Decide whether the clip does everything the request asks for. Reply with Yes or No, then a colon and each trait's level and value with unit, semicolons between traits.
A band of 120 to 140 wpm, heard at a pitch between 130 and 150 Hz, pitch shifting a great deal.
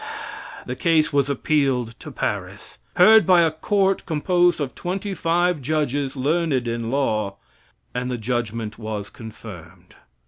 Yes: slow, 135 wpm; medium, 140 Hz; wide, 6.4 semitones